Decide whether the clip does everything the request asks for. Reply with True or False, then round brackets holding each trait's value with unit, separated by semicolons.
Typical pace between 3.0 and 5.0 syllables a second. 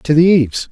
False (6.0 syllables/s)